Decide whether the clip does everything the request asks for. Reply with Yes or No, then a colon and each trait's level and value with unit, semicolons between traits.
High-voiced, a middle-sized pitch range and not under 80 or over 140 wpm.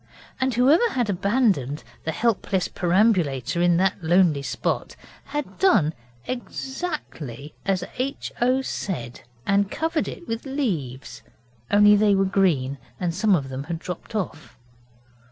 No: high, 195 Hz; wide, 7.2 semitones; slow, 135 wpm